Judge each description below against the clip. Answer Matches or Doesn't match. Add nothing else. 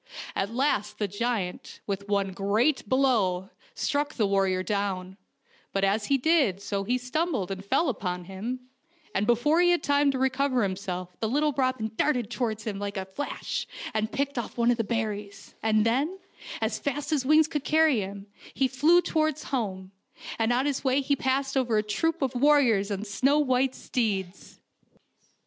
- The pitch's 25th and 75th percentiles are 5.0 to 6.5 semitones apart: Matches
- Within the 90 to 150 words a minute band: Doesn't match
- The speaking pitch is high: Matches